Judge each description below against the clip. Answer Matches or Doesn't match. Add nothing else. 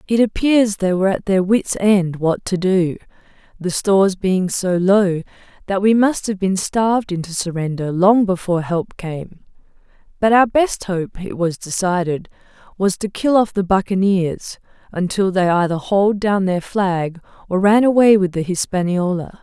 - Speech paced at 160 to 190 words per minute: Matches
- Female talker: Matches